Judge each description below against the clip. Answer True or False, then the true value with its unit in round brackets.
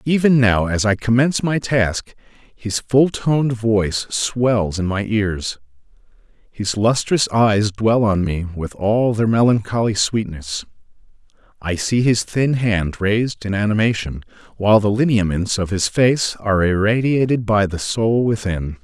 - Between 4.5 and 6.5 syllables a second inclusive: False (4.3 syllables/s)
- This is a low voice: True (110 Hz)